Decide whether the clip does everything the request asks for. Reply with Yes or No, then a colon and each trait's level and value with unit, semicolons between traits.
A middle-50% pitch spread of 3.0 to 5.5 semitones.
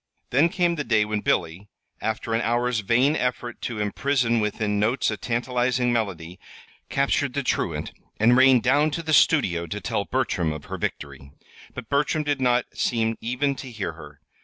Yes: average, 4.2 semitones